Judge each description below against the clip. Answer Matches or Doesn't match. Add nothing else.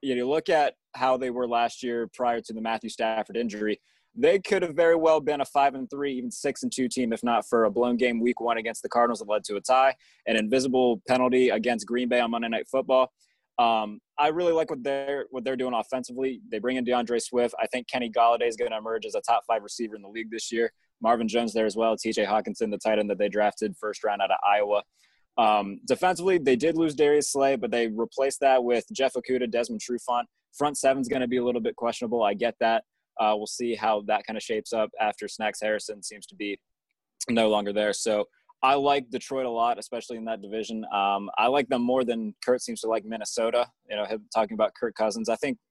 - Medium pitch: Doesn't match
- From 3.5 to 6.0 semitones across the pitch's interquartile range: Doesn't match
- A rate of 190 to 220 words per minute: Doesn't match